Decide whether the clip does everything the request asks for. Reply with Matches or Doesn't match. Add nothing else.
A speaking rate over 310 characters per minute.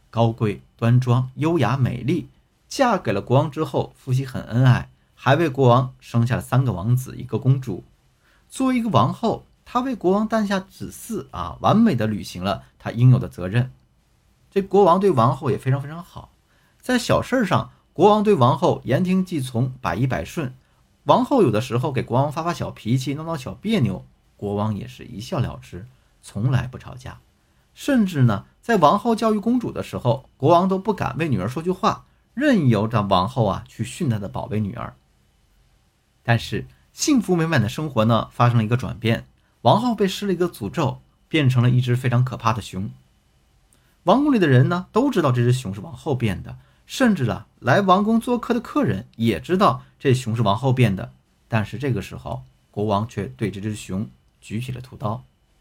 Doesn't match